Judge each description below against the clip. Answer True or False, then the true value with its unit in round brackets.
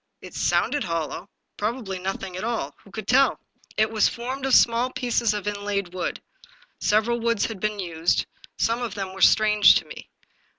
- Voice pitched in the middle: False (210 Hz)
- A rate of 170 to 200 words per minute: True (180 wpm)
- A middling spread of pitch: True (3.4 semitones)